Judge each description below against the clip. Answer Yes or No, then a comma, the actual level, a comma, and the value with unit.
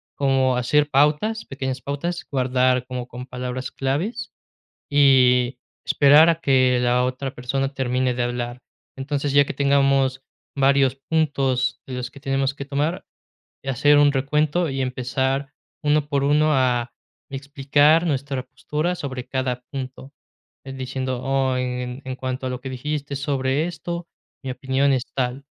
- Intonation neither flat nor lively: No, narrow, 2.0 semitones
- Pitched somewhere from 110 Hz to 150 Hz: Yes, low, 135 Hz